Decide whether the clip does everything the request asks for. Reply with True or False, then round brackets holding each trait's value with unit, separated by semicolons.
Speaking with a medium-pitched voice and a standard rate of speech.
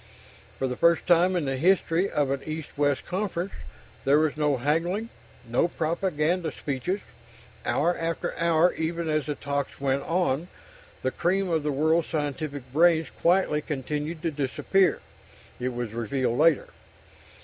True (155 Hz; 150 wpm)